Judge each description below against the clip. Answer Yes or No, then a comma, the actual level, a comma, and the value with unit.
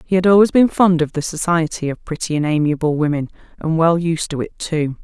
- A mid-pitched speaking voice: Yes, medium, 160 Hz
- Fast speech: Yes, fast, 225 wpm